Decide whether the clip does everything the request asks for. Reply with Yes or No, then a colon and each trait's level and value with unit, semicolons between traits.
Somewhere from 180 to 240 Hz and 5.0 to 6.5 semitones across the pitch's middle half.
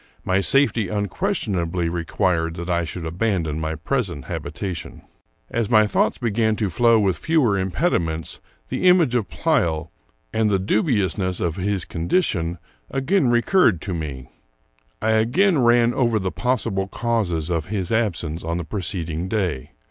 No: very low, 95 Hz; wide, 5.6 semitones